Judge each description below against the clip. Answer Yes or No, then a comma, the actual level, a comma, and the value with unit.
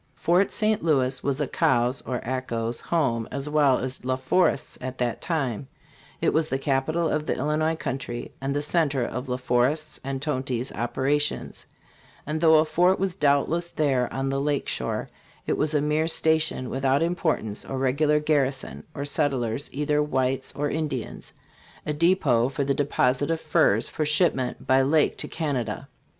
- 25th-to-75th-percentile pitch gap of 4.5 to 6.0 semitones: No, average, 3.1 semitones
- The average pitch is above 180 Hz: No, medium, 140 Hz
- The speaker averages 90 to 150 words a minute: No, average, 165 wpm